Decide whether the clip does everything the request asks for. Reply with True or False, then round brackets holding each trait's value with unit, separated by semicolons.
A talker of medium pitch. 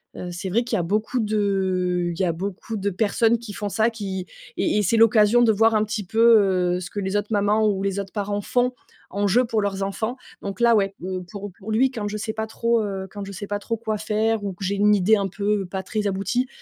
False (205 Hz)